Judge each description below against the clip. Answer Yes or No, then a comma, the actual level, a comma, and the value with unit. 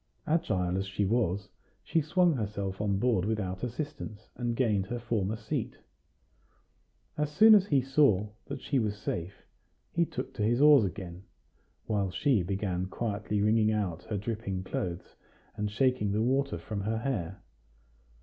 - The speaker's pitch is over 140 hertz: No, low, 105 Hz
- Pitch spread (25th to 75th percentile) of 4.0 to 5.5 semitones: Yes, average, 4.7 semitones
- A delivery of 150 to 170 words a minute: Yes, average, 155 wpm